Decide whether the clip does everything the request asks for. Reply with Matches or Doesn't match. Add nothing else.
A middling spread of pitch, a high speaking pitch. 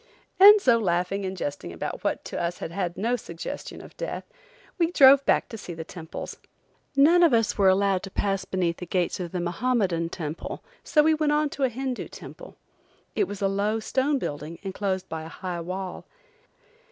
Doesn't match